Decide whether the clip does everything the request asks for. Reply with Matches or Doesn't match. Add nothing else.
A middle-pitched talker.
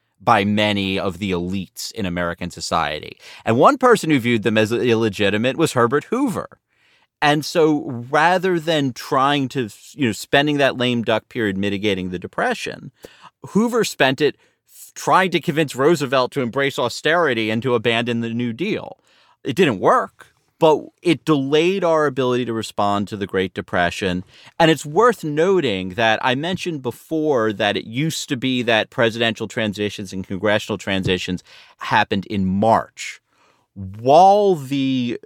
Doesn't match